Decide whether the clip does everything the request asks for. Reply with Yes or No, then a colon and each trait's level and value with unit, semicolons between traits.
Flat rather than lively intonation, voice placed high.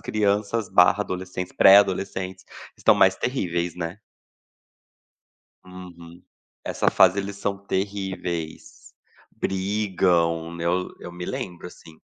No: narrow, 2.3 semitones; very low, 95 Hz